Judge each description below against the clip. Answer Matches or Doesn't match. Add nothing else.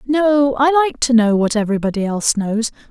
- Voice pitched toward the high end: Matches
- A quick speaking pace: Doesn't match